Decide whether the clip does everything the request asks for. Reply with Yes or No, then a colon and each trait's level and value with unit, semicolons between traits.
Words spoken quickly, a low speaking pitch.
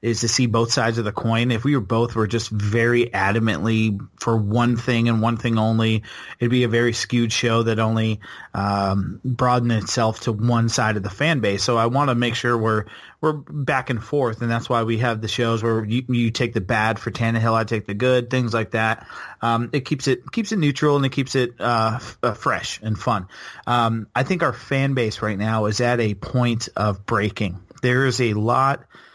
Yes: fast, 220 wpm; low, 115 Hz